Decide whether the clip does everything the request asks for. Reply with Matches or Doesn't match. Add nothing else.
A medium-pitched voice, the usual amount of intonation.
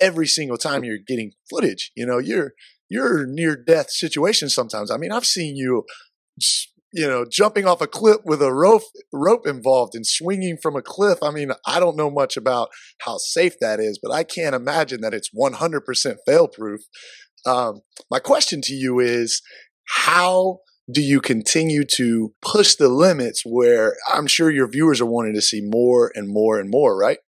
Doesn't match